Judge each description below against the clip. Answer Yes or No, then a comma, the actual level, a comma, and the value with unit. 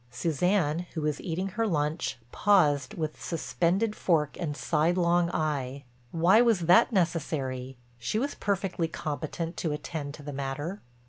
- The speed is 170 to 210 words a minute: No, slow, 135 wpm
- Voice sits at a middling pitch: Yes, medium, 160 Hz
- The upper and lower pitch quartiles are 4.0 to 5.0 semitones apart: No, average, 3.6 semitones